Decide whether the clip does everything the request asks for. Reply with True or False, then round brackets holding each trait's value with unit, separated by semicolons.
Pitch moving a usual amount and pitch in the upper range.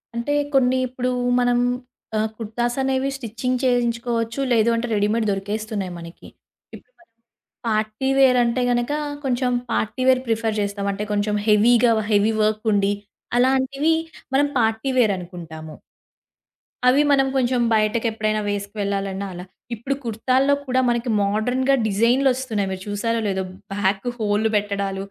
True (3.6 semitones; 225 Hz)